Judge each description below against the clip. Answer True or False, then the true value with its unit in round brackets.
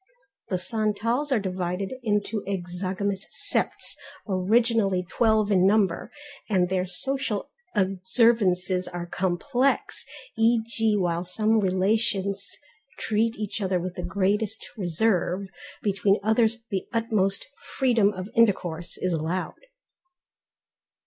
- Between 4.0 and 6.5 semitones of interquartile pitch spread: False (3.3 semitones)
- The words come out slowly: True (105 wpm)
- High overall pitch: True (200 Hz)